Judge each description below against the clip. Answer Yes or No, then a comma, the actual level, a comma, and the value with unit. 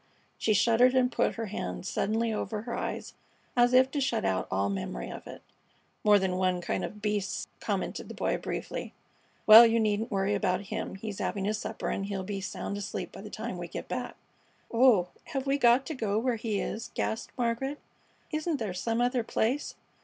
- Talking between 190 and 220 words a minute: Yes, average, 200 wpm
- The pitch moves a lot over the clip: No, average, 3.6 semitones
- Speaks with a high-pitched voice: Yes, high, 220 Hz